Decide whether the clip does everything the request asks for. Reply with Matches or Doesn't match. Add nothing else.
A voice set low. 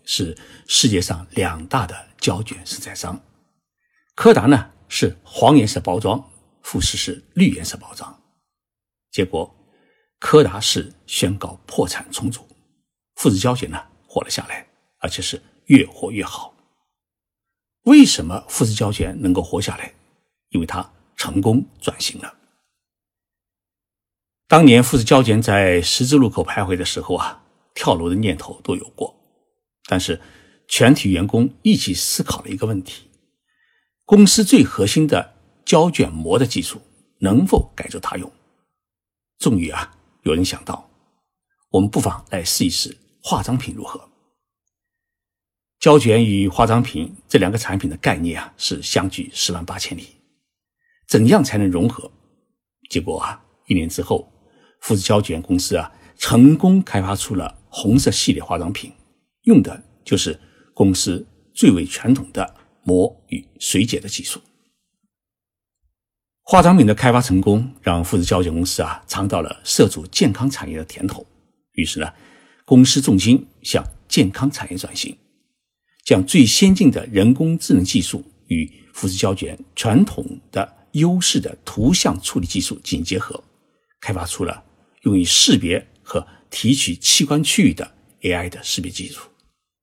Matches